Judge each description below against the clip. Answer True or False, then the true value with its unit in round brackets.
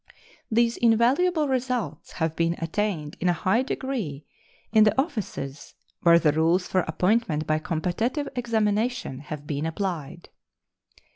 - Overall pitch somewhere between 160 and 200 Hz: True (190 Hz)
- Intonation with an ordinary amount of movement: False (6.9 semitones)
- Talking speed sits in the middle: False (130 wpm)